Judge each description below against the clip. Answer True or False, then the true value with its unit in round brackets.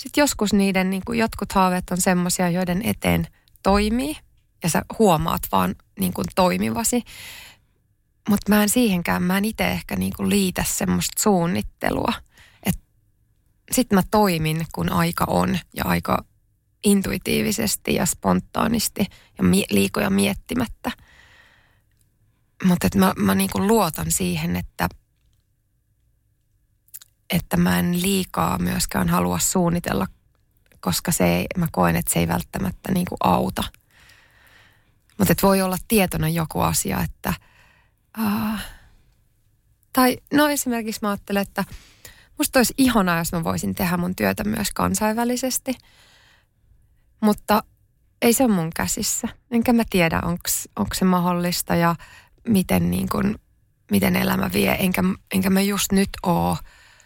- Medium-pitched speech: True (180 Hz)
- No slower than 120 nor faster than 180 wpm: True (130 wpm)